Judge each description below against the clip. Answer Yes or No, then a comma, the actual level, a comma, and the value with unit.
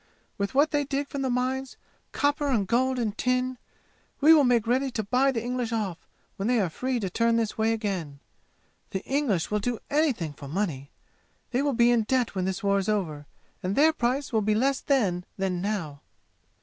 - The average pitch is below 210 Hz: No, high, 230 Hz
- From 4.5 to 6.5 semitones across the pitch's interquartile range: Yes, average, 4.9 semitones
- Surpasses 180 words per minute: Yes, average, 200 wpm